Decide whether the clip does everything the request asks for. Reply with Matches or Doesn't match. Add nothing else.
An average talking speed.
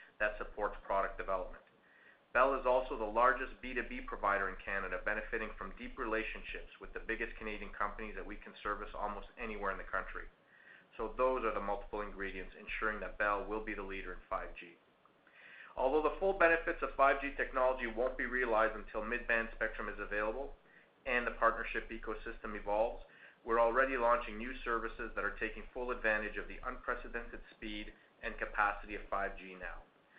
Matches